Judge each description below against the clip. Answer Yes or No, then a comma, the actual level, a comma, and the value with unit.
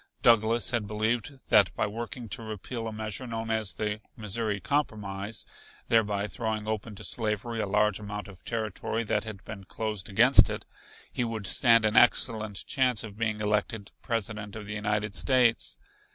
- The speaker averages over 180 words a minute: No, average, 165 wpm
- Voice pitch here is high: No, low, 110 Hz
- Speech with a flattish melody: Yes, narrow, 1.8 semitones